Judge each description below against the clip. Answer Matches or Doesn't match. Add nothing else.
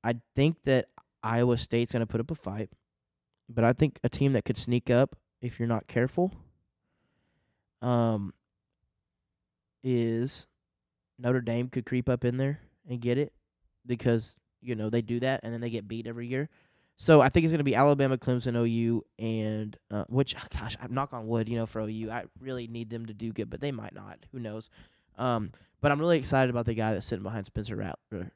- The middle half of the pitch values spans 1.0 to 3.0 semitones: Matches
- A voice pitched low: Matches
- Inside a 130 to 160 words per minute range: Doesn't match